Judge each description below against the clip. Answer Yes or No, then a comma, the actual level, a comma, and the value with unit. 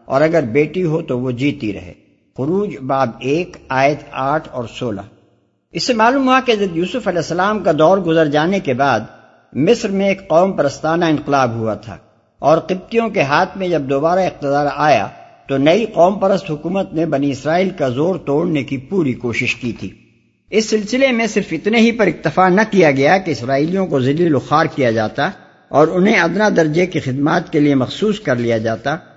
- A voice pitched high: No, medium, 160 Hz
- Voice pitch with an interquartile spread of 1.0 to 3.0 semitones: No, average, 5.3 semitones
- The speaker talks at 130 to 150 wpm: No, fast, 190 wpm